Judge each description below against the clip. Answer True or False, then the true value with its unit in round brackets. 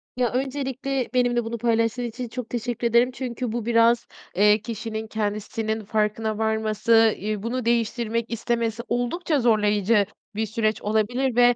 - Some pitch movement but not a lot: False (1.9 semitones)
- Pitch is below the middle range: False (230 Hz)